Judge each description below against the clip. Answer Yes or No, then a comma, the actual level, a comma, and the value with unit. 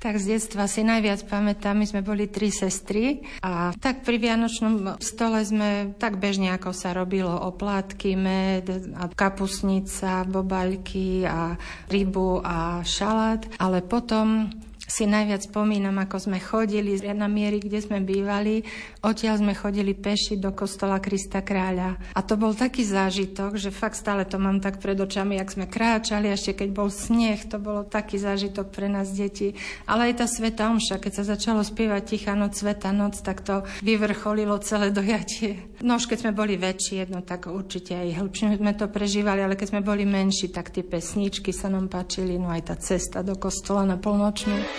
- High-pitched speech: Yes, high, 200 Hz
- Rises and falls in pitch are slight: Yes, narrow, 1.7 semitones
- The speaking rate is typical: No, fast, 175 wpm